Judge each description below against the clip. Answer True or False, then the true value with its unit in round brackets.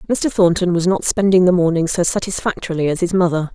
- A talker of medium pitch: True (180 Hz)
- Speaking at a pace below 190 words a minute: False (205 wpm)